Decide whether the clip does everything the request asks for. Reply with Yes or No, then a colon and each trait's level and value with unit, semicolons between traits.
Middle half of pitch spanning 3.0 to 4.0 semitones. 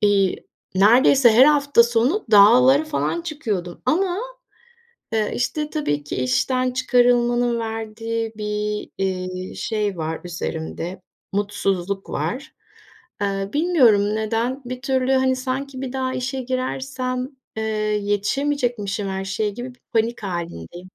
No: average, 4.5 semitones